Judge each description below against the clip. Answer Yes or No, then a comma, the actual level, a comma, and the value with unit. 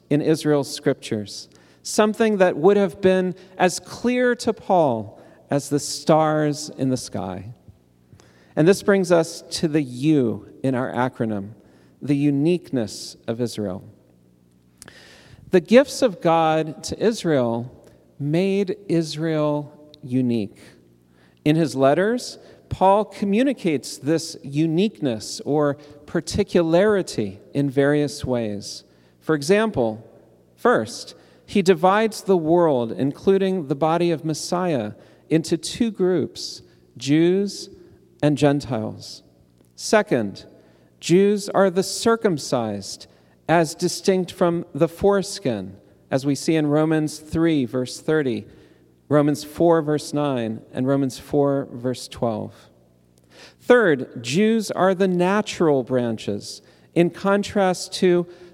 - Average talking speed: No, slow, 110 wpm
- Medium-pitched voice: Yes, medium, 150 Hz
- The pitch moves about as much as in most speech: No, wide, 7.3 semitones